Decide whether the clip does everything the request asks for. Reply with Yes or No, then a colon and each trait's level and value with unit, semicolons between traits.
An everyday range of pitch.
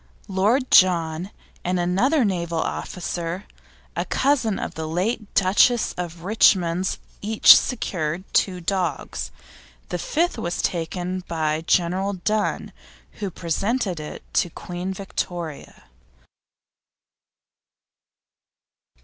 Yes: average, 3.1 semitones